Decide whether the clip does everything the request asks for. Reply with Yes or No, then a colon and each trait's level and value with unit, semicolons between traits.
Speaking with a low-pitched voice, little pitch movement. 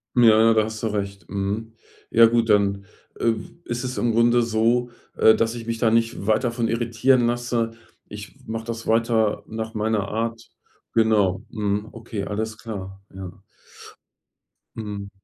Yes: low, 110 Hz; narrow, 2.0 semitones